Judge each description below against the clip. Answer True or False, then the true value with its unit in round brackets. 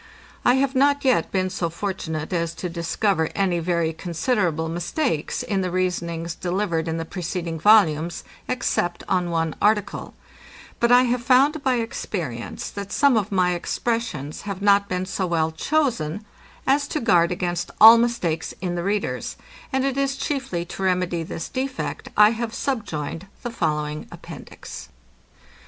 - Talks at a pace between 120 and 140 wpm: False (155 wpm)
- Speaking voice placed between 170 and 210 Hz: True (185 Hz)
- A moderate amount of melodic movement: False (5.7 semitones)